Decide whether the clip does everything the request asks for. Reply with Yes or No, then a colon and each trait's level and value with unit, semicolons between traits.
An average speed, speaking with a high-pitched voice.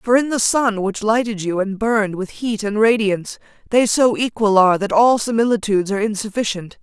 Yes: average, 195 wpm; high, 215 Hz